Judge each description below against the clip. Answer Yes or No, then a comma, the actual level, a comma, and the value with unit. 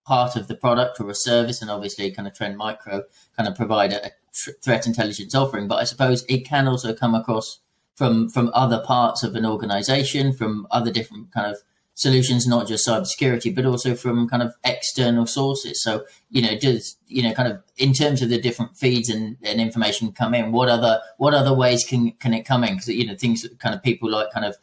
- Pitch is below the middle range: Yes, low, 120 Hz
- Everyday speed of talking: No, fast, 225 wpm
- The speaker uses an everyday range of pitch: No, narrow, 2.2 semitones